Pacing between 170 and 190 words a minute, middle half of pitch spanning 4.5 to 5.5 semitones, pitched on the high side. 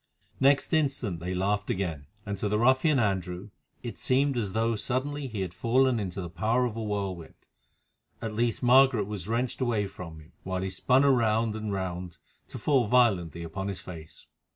No: average, 180 wpm; average, 5.1 semitones; low, 105 Hz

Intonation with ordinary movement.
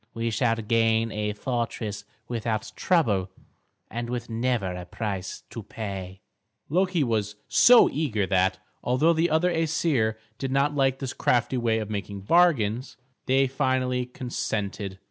Yes: average, 4.2 semitones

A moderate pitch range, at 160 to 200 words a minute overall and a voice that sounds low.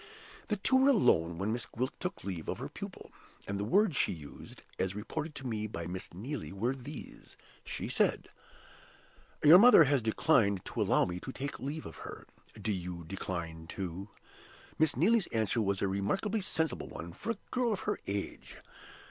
No: wide, 9.0 semitones; average, 180 wpm; low, 110 Hz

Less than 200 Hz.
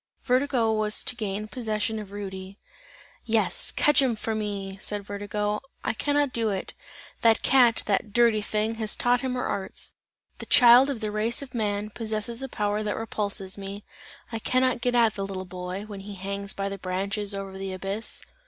No: high, 210 Hz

